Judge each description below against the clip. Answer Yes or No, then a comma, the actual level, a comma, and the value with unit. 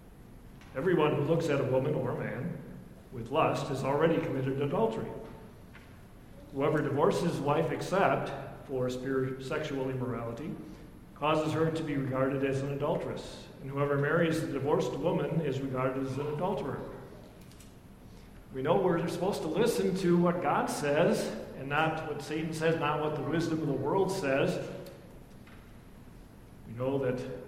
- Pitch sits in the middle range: Yes, medium, 145 Hz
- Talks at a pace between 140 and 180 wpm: Yes, average, 150 wpm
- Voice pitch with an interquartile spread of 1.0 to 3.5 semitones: Yes, average, 3.0 semitones